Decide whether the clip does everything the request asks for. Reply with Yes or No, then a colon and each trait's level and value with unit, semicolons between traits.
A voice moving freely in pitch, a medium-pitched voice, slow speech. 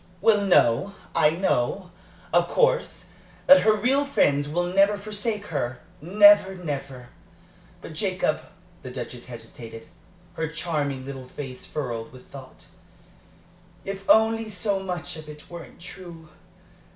Yes: wide, 6.6 semitones; medium, 170 Hz; slow, 125 wpm